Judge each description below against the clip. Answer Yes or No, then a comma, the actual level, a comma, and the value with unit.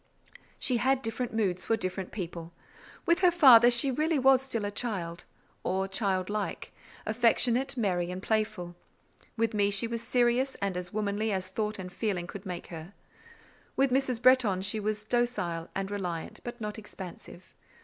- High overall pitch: Yes, high, 215 Hz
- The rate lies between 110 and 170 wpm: Yes, average, 165 wpm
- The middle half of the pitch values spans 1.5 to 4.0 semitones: No, average, 4.4 semitones